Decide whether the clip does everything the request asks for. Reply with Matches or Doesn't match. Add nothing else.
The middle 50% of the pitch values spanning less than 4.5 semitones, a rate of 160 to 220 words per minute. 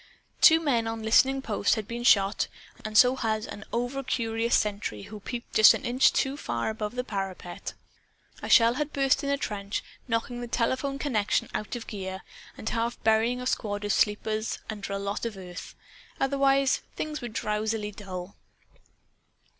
Matches